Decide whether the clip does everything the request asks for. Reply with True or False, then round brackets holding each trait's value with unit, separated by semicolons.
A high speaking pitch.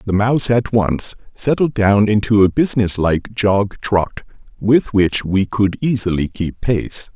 False (105 Hz)